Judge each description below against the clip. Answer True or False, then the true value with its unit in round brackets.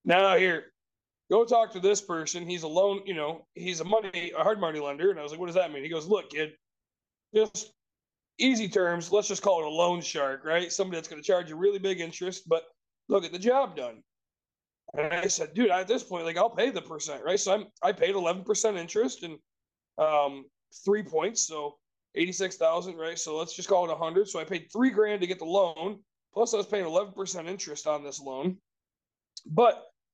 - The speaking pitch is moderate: True (180 Hz)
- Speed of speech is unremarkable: False (220 wpm)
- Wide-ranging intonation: False (4.0 semitones)